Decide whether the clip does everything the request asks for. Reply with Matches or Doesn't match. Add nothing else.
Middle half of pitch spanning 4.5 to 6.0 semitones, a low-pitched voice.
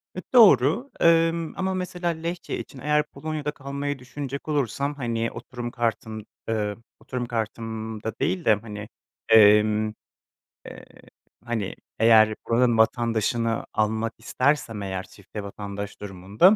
Matches